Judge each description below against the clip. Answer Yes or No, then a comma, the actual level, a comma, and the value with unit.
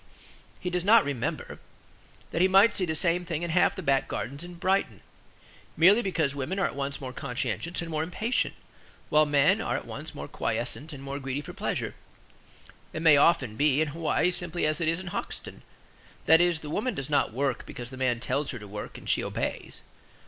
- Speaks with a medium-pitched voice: Yes, medium, 155 Hz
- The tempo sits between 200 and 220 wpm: Yes, fast, 205 wpm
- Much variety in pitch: No, average, 4.3 semitones